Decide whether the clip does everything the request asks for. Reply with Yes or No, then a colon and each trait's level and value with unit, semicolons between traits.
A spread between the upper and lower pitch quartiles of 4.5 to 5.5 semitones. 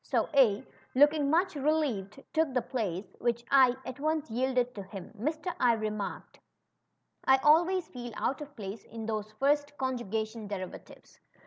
Yes: average, 5.2 semitones